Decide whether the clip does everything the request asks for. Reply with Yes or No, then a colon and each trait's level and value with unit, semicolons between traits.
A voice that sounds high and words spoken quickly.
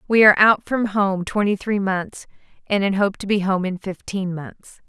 Yes: high, 195 Hz; fast, 210 wpm